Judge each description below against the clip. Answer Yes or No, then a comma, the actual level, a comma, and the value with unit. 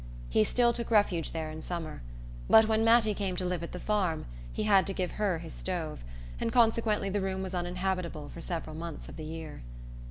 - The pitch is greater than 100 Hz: Yes, medium, 185 Hz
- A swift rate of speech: Yes, fast, 210 wpm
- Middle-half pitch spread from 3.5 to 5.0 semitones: Yes, average, 4.3 semitones